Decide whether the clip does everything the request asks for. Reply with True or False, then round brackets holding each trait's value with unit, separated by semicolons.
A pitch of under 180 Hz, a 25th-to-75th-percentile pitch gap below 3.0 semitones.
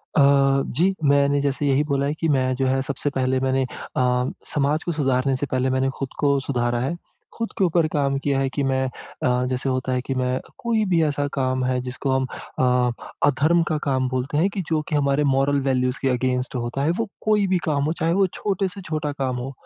True (140 Hz; 2.6 semitones)